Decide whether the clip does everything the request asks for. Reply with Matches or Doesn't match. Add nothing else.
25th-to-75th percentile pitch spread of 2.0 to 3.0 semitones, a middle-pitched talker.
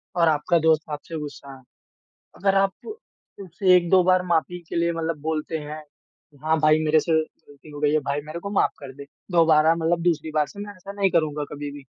Matches